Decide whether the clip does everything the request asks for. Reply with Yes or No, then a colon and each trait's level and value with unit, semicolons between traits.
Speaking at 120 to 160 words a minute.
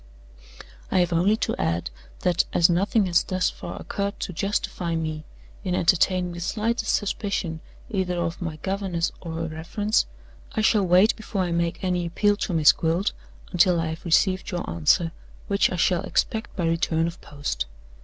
No: average, 175 wpm